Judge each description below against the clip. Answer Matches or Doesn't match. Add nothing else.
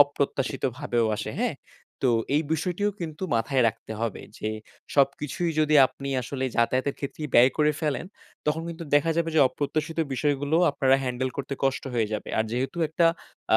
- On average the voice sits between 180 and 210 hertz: Doesn't match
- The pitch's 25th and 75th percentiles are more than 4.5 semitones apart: Doesn't match